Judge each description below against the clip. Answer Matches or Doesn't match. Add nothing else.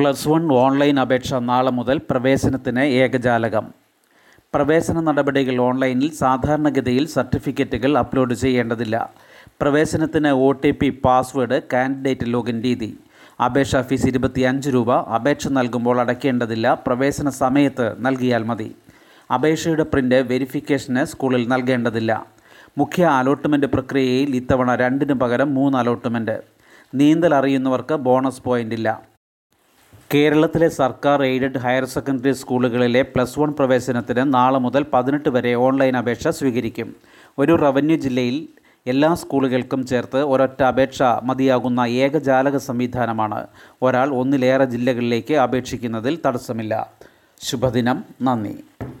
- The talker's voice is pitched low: Matches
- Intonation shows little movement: Matches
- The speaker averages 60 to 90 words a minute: Doesn't match